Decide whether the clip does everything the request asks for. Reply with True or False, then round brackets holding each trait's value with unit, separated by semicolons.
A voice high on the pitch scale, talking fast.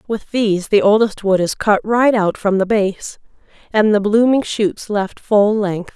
False (210 Hz; 190 wpm)